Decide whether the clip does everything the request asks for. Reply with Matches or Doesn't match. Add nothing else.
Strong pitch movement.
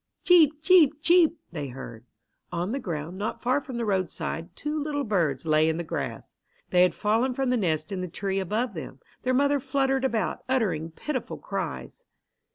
Matches